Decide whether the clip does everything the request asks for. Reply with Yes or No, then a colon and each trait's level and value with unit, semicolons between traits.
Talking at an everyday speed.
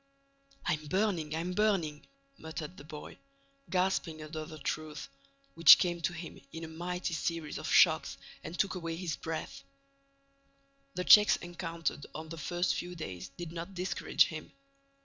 Yes: average, 150 wpm